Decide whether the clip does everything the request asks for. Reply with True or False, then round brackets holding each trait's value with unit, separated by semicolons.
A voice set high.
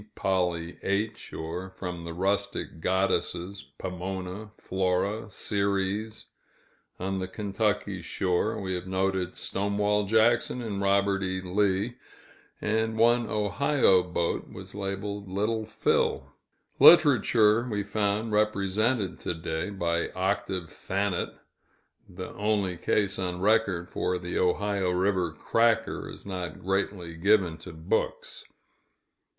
False (95 Hz)